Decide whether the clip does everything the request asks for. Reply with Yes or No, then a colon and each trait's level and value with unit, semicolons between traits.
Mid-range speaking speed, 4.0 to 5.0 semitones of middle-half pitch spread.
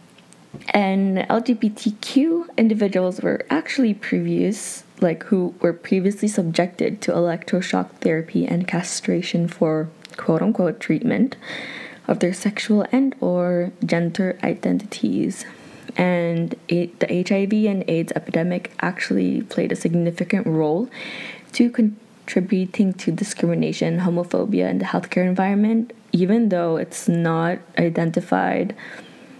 No: slow, 105 wpm; average, 4.5 semitones